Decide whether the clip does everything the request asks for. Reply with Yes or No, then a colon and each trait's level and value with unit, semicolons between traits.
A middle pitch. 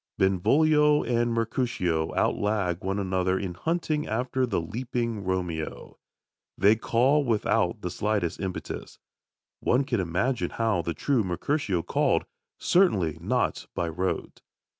No: low, 105 Hz